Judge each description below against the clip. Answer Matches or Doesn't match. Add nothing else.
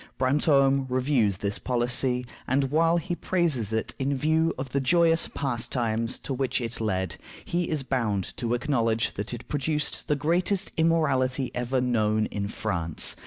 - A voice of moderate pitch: Doesn't match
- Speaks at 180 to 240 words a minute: Doesn't match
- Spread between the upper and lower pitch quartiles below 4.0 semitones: Doesn't match